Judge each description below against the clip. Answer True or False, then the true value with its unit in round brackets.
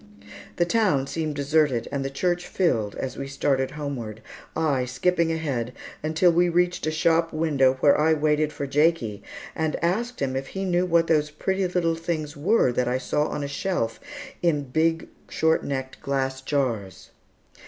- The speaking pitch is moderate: True (150 Hz)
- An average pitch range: True (3.9 semitones)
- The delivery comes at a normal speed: True (170 wpm)